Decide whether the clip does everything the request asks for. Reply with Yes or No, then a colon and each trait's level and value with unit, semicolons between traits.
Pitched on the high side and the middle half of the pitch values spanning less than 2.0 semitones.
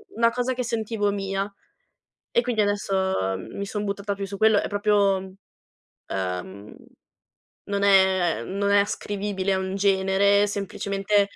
Yes: high, 200 Hz; narrow, 1.2 semitones